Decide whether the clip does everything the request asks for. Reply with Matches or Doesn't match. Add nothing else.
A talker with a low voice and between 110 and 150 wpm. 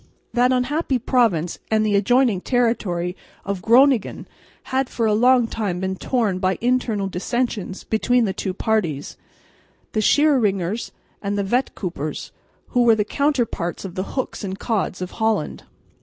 Doesn't match